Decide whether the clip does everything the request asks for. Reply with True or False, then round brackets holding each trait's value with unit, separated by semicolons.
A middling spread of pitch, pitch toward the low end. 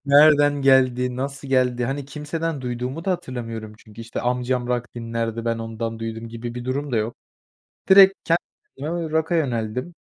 True (3.9 semitones; 125 Hz)